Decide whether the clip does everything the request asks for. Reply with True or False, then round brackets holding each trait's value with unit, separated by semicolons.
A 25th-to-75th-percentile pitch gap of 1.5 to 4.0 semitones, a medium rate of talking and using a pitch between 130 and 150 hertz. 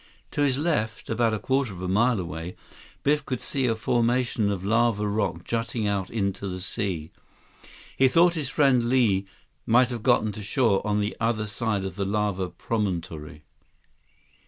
False (3.7 semitones; 170 wpm; 110 Hz)